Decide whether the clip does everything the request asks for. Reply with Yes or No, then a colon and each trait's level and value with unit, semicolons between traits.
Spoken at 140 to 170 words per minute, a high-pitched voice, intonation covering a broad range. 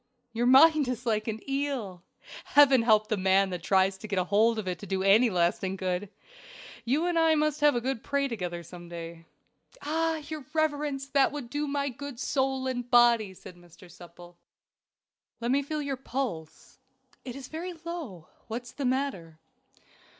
No: average, 185 wpm; high, 240 Hz; wide, 6.9 semitones